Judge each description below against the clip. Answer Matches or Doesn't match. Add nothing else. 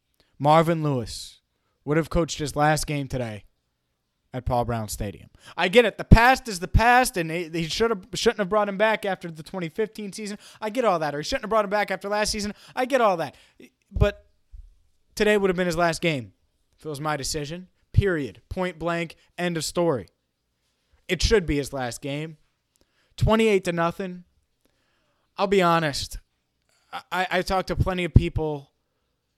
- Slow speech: Doesn't match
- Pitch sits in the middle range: Matches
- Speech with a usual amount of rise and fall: Doesn't match